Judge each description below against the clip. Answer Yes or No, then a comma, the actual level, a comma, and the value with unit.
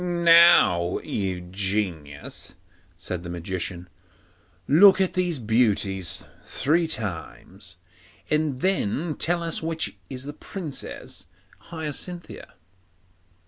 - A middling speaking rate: No, slow, 95 wpm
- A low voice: Yes, low, 130 Hz